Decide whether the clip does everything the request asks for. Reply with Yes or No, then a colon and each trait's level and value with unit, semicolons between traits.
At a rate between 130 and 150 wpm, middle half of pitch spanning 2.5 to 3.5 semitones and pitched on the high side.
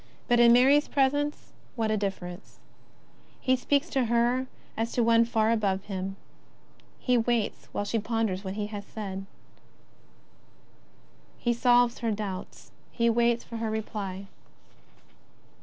Yes: slow, 135 wpm; average, 2.9 semitones; high, 230 Hz